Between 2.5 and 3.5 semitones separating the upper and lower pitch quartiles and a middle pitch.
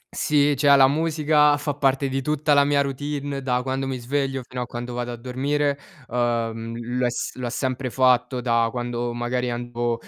No: average, 2.8 semitones; low, 130 Hz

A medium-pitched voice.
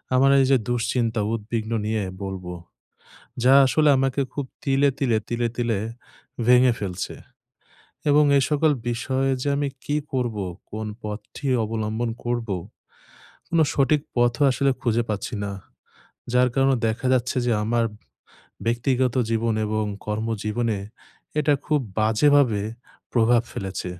No: low, 120 Hz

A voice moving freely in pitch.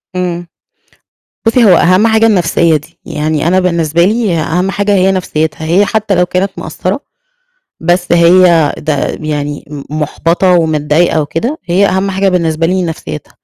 No: average, 3.1 semitones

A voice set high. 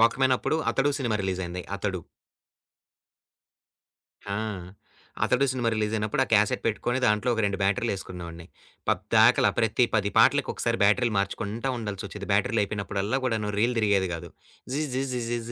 No: low, 105 Hz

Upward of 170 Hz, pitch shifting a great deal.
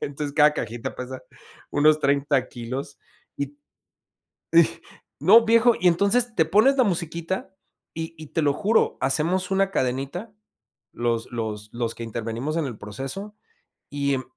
No: medium, 145 Hz; wide, 6.4 semitones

